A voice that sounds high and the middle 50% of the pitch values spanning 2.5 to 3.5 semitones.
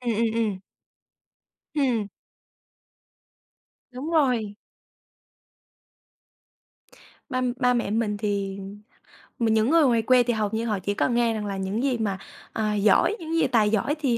Yes: high, 225 Hz; average, 3.2 semitones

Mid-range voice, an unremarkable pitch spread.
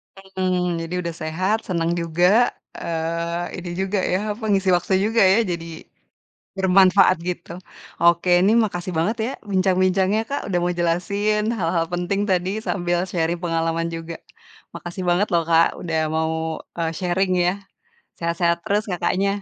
No: medium, 180 Hz; narrow, 2.2 semitones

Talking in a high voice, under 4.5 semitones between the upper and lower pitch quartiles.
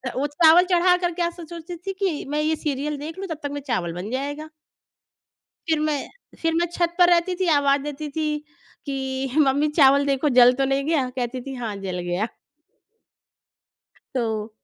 Yes: very high, 290 Hz; average, 3.8 semitones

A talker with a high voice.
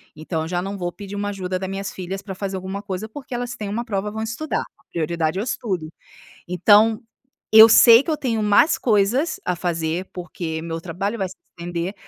Yes: high, 195 Hz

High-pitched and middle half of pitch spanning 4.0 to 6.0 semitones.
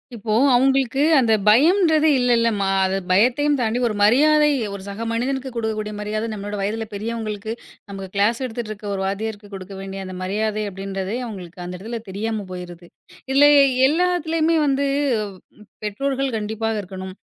Yes: high, 220 Hz; average, 4.5 semitones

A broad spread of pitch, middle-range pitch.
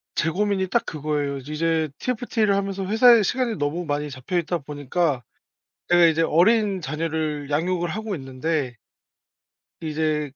No: average, 4.6 semitones; medium, 165 Hz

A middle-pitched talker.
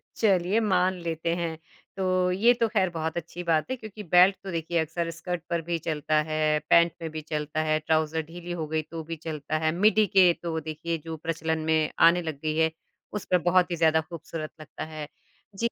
Yes: medium, 165 Hz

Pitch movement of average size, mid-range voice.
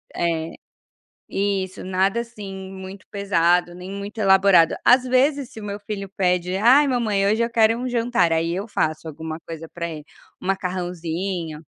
No: average, 3.9 semitones; high, 195 Hz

